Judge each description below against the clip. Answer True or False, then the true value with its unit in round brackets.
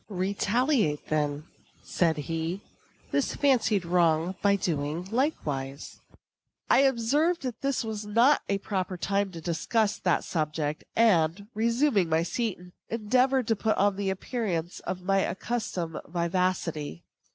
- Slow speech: True (130 wpm)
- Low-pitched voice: False (195 Hz)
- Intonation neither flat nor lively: False (5.7 semitones)